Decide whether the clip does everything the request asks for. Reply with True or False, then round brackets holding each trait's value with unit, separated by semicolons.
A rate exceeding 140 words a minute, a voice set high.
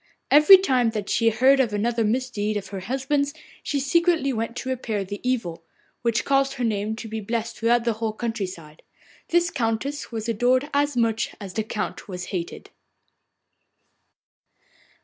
True (165 wpm; 230 Hz)